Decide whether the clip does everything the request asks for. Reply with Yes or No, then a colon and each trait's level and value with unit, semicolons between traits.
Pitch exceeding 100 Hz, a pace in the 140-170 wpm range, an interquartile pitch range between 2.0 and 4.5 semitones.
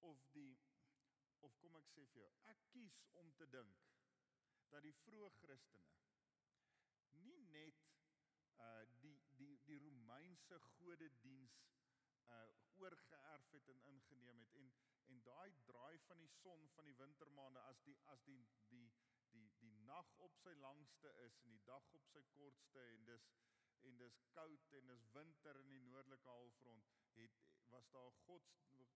Yes: low, 135 Hz; average, 160 wpm; average, 3.9 semitones